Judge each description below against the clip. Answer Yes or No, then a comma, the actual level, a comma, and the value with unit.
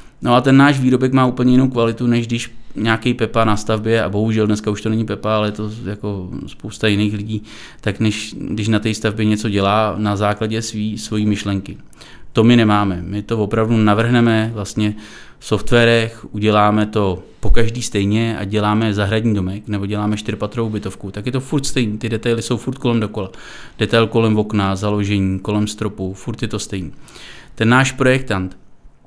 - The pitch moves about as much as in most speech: No, narrow, 1.8 semitones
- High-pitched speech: No, low, 110 Hz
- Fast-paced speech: Yes, fast, 185 wpm